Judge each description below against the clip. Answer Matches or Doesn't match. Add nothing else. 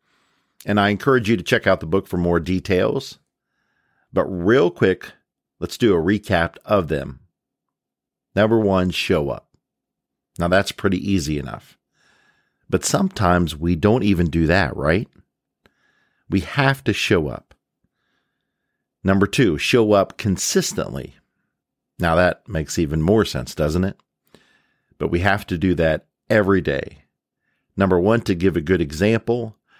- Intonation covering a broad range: Doesn't match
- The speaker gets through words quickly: Doesn't match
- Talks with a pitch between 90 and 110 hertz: Matches